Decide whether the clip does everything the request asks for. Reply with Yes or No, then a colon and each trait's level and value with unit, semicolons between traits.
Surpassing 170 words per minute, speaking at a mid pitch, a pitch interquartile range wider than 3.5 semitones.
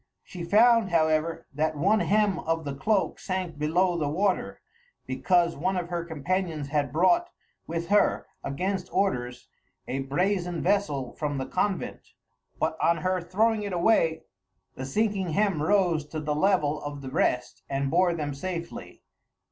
No: average, 155 wpm; medium, 170 Hz; average, 4.3 semitones